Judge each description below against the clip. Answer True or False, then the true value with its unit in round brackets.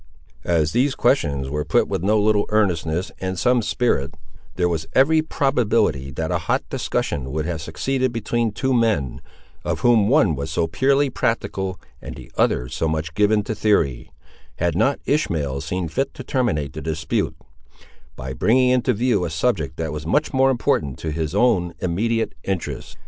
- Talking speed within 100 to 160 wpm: False (170 wpm)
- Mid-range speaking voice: False (95 Hz)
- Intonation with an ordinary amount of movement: False (7.2 semitones)